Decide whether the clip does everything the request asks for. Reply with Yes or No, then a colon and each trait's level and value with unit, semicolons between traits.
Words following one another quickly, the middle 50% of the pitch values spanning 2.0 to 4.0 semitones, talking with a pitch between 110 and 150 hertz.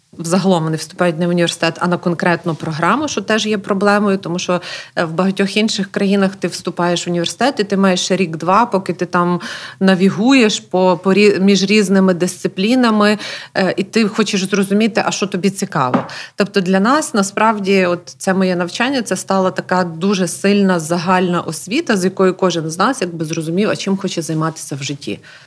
No: fast, 175 wpm; narrow, 2.5 semitones; high, 190 Hz